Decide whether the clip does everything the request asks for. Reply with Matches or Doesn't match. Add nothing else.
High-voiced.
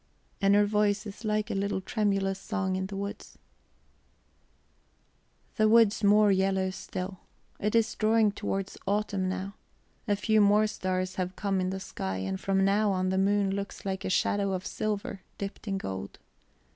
Matches